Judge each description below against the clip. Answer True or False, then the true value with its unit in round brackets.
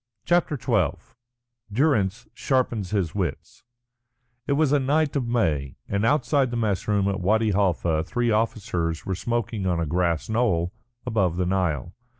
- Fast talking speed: False (155 wpm)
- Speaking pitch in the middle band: False (105 Hz)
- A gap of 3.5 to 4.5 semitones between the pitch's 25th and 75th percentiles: False (5.2 semitones)